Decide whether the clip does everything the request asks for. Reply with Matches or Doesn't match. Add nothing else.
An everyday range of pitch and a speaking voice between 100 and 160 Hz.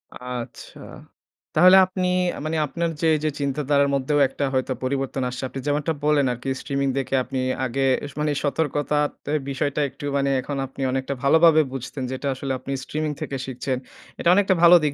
Doesn't match